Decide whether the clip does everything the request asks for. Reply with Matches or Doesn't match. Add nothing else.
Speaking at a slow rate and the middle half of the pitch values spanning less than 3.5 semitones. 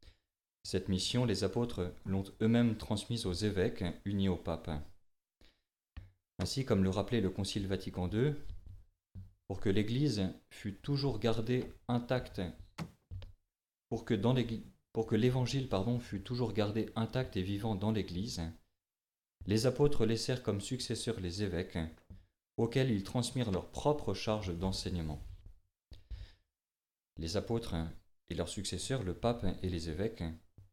Doesn't match